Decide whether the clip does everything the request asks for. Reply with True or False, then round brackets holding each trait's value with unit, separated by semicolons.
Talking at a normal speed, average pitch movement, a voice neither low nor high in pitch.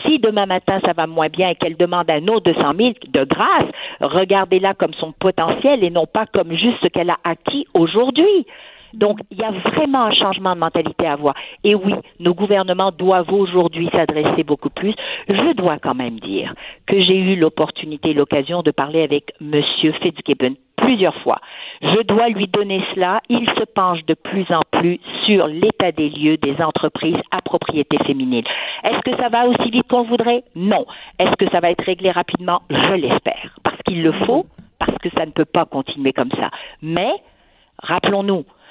True (190 wpm; 4.3 semitones; 180 Hz)